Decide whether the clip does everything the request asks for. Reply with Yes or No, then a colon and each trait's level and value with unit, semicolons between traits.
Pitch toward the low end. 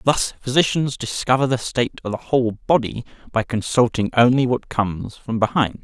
Yes: low, 120 Hz